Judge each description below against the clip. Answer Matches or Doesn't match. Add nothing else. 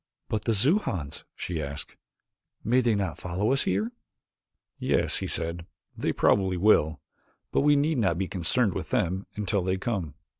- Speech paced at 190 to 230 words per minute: Doesn't match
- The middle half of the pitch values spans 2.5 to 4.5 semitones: Doesn't match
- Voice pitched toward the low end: Matches